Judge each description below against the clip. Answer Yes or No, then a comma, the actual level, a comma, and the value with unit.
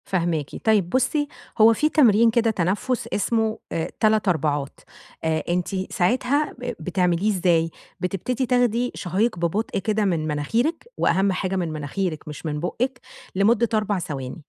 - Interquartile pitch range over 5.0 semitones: Yes, wide, 5.5 semitones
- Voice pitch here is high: Yes, high, 195 Hz